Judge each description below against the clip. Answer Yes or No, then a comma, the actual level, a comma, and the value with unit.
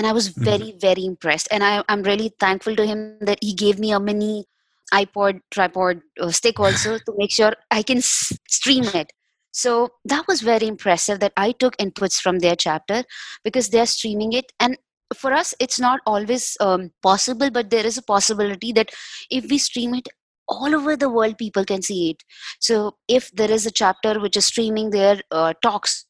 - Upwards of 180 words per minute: Yes, average, 200 wpm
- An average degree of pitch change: Yes, average, 3.3 semitones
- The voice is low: No, high, 215 Hz